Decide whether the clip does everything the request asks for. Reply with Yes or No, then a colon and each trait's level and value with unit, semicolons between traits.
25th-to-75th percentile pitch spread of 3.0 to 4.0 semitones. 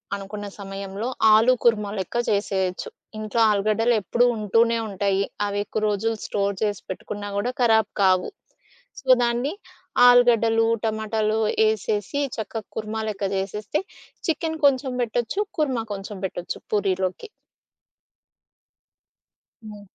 No: narrow, 2.5 semitones